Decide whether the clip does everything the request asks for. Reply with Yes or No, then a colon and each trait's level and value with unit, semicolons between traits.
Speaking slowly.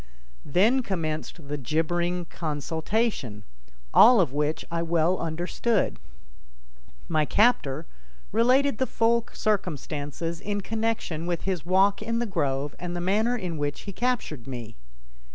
Yes: slow, 130 wpm